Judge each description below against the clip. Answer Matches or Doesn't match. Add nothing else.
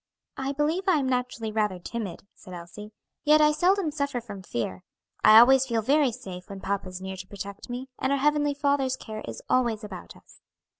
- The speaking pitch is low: Doesn't match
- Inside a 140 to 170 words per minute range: Doesn't match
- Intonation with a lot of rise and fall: Matches